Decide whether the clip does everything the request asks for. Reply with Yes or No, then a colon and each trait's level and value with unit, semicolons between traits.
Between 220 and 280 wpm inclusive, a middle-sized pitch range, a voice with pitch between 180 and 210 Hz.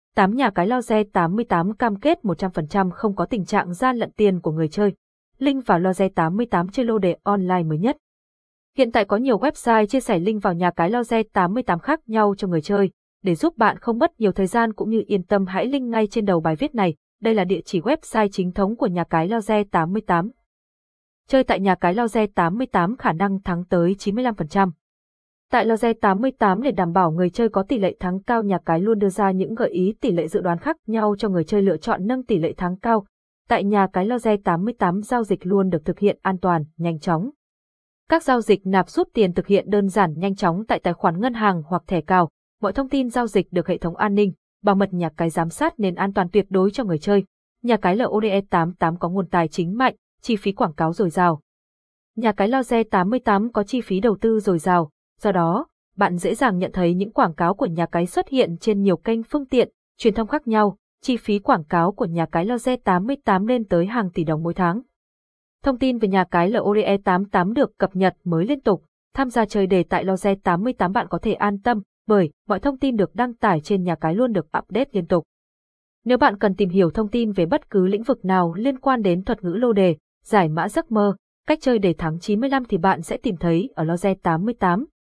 Yes: average, 235 wpm; average, 4.4 semitones; high, 200 Hz